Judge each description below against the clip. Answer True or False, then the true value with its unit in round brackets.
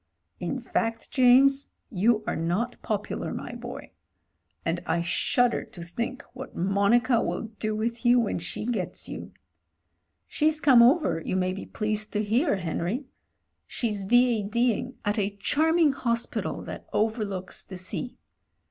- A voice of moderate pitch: False (225 Hz)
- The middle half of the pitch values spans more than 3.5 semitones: True (3.9 semitones)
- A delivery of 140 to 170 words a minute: True (155 wpm)